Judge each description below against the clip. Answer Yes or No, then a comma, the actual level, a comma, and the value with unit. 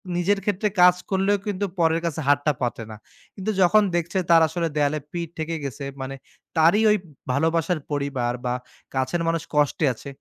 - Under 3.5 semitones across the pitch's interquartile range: No, average, 3.9 semitones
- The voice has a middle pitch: Yes, medium, 165 Hz